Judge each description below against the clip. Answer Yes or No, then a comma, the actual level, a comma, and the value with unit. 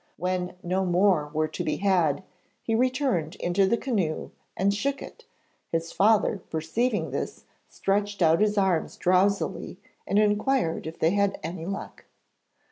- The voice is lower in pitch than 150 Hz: No, high, 190 Hz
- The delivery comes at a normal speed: Yes, average, 150 wpm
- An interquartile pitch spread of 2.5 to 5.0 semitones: Yes, average, 3.9 semitones